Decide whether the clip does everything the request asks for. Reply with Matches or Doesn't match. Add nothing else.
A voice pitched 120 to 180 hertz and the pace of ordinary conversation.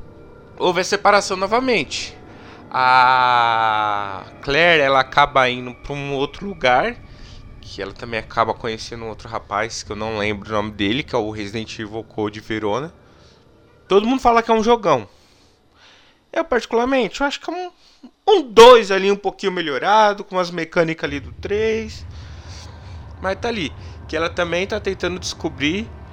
Matches